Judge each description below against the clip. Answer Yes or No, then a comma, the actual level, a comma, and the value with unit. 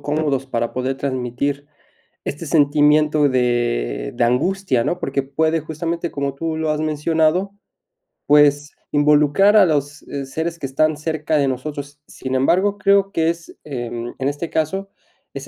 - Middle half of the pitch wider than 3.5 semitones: No, average, 3.0 semitones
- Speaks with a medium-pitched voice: Yes, medium, 150 Hz